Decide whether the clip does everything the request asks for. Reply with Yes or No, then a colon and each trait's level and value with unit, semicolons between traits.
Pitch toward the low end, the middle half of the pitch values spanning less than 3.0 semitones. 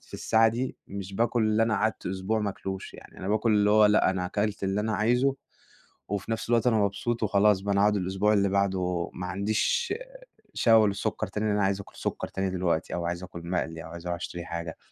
Yes: low, 100 Hz; narrow, 2.6 semitones